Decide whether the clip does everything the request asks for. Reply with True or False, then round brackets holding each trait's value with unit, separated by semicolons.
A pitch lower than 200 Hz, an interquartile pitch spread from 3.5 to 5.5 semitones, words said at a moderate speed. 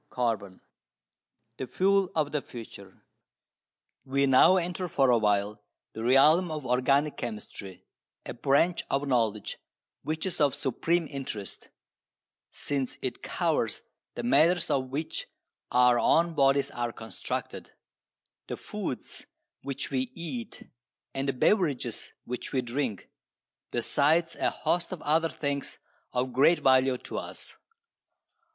False (135 Hz; 4.3 semitones; 130 wpm)